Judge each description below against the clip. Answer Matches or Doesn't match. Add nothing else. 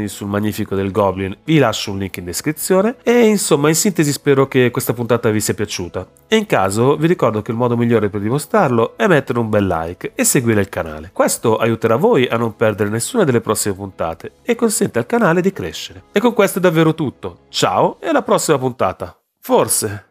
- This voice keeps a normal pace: Doesn't match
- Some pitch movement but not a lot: Doesn't match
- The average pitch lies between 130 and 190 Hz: Doesn't match